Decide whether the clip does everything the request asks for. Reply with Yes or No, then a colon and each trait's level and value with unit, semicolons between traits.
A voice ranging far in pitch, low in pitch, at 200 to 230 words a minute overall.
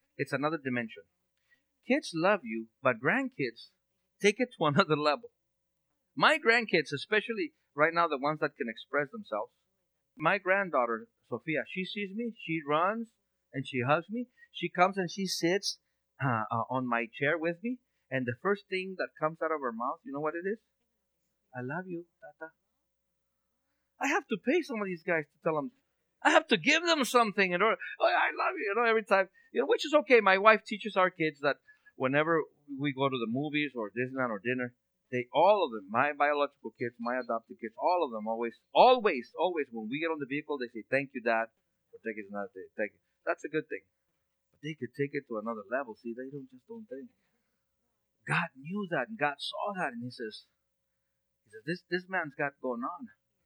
No: wide, 8.4 semitones; medium, 160 Hz; fast, 205 wpm